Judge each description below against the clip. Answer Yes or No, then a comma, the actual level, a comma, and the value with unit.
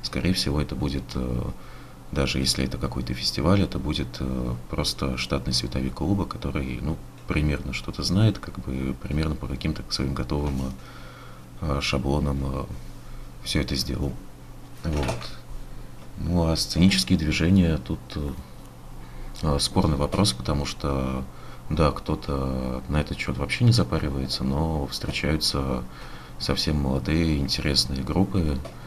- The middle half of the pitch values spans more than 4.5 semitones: No, average, 3.5 semitones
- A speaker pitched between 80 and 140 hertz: No, very low, 70 Hz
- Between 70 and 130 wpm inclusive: Yes, average, 115 wpm